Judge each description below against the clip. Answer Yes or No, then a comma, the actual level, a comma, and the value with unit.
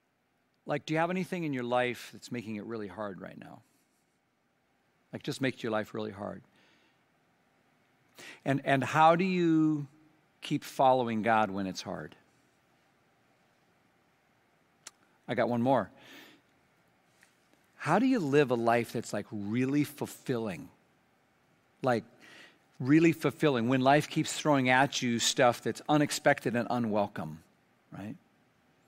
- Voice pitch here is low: Yes, low, 130 Hz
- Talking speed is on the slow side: Yes, slow, 130 wpm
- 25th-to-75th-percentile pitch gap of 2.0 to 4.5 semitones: No, average, 5.1 semitones